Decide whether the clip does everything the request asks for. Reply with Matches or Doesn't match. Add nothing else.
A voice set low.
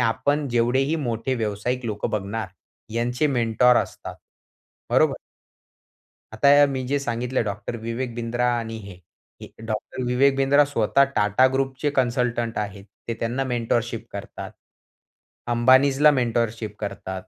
Matches